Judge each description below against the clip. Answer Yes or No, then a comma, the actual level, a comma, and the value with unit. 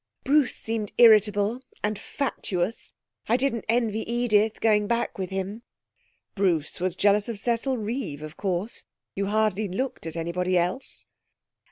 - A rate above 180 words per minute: No, average, 140 wpm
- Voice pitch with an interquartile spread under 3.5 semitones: No, average, 3.8 semitones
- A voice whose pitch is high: Yes, high, 210 Hz